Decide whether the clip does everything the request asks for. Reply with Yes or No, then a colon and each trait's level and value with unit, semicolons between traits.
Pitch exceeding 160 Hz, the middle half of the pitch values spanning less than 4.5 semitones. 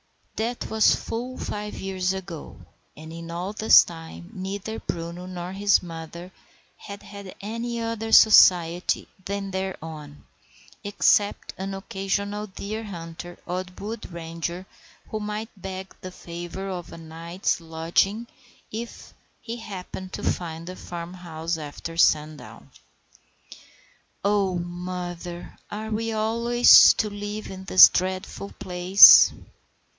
Yes: medium, 185 Hz; average, 3.3 semitones